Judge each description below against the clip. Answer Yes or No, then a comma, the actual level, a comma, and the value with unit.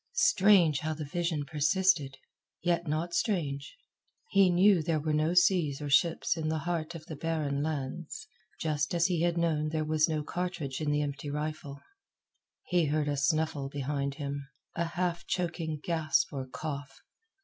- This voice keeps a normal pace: Yes, average, 165 wpm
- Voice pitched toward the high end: No, medium, 155 Hz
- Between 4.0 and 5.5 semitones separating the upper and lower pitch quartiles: No, average, 2.9 semitones